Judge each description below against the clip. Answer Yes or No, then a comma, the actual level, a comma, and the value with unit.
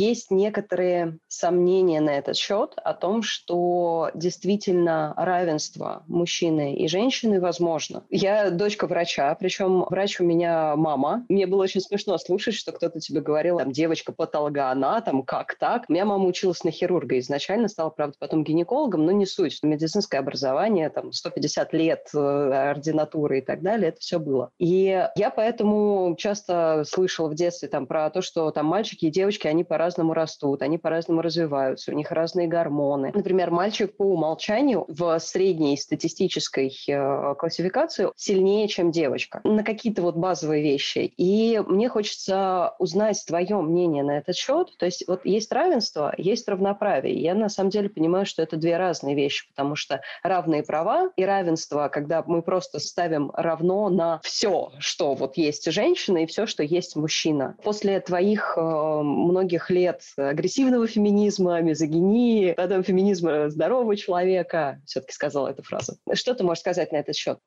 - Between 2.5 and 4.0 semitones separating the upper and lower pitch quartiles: Yes, average, 3.7 semitones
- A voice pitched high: No, medium, 175 Hz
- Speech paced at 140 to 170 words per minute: Yes, average, 155 wpm